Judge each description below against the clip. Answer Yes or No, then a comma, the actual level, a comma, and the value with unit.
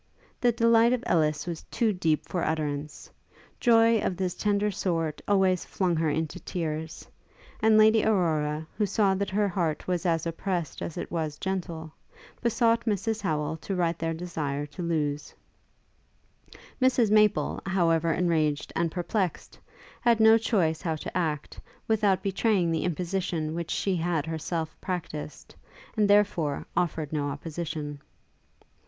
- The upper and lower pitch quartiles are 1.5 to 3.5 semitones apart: No, average, 4.3 semitones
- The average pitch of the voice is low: No, medium, 175 Hz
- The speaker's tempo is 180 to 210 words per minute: No, average, 145 wpm